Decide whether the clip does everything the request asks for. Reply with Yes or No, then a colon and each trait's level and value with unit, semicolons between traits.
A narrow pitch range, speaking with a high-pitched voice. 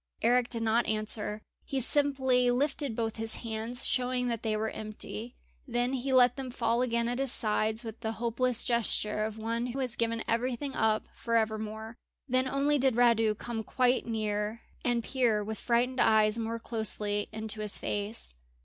Yes: narrow, 2.2 semitones; high, 230 Hz